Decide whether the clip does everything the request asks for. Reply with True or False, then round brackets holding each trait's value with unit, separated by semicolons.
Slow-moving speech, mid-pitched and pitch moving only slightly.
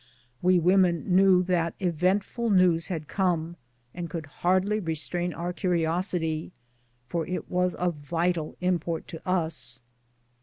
True (125 wpm; 175 Hz; 2.0 semitones)